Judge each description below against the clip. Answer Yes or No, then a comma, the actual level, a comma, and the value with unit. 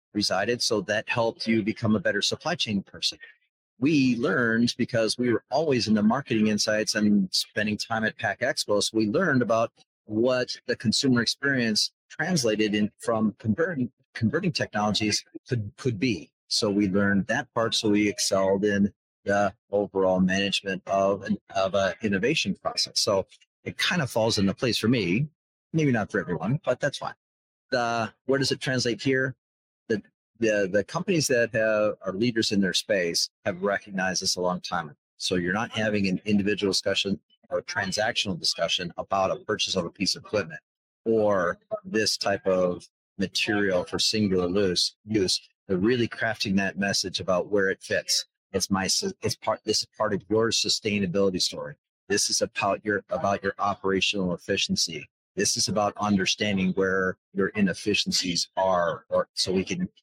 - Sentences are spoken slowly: No, average, 165 wpm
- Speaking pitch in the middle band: No, low, 105 Hz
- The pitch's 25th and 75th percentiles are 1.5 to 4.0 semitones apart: Yes, average, 3.0 semitones